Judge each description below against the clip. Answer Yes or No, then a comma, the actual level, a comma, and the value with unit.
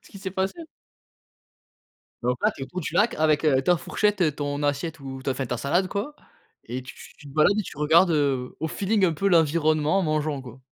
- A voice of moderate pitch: Yes, medium, 155 Hz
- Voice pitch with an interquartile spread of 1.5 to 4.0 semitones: No, average, 5.0 semitones